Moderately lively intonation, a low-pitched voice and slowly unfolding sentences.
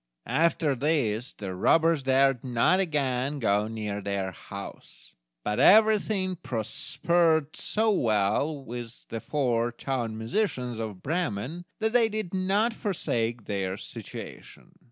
No: wide, 7.6 semitones; low, 130 Hz; slow, 120 wpm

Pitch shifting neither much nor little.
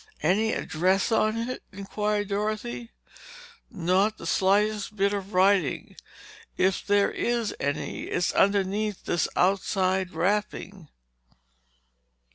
No: narrow, 2.2 semitones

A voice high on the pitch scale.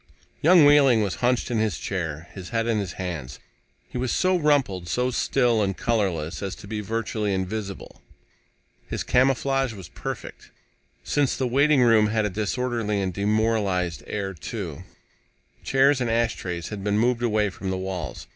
No: low, 110 Hz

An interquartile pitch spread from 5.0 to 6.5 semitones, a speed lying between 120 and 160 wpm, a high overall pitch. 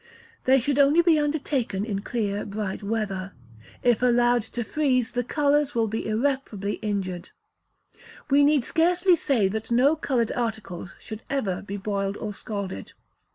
Yes: wide, 5.5 semitones; average, 150 wpm; high, 230 Hz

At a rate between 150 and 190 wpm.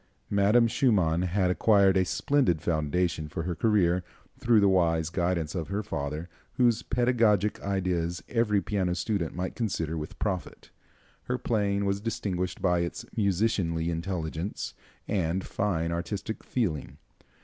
No: slow, 135 wpm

